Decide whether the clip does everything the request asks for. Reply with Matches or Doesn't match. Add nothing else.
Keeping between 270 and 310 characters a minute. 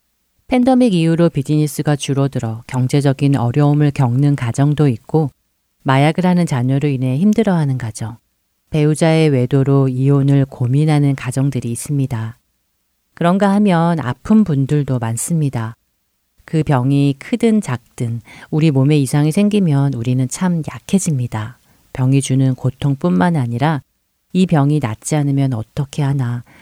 Matches